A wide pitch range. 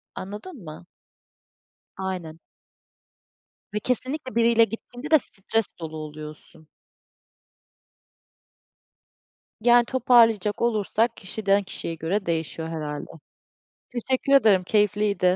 Yes: wide, 5.9 semitones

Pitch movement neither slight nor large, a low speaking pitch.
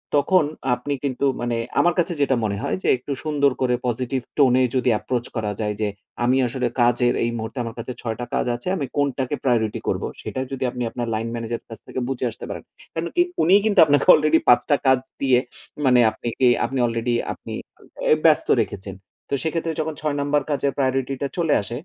Yes: average, 3.3 semitones; low, 130 Hz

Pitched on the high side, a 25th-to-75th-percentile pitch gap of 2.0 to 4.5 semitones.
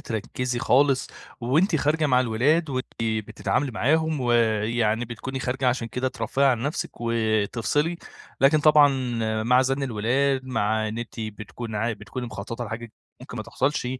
No: low, 125 Hz; average, 3.4 semitones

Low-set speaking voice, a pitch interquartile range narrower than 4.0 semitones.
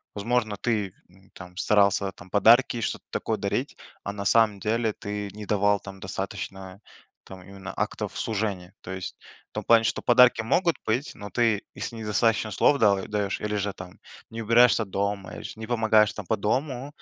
Yes: low, 105 Hz; narrow, 2.5 semitones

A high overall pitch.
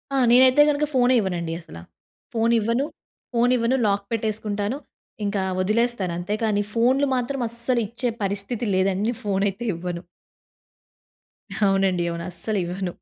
Yes: high, 215 Hz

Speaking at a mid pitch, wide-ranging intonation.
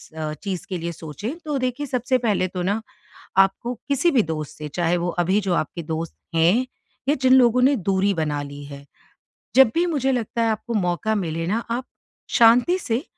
No: high, 205 Hz; wide, 7.0 semitones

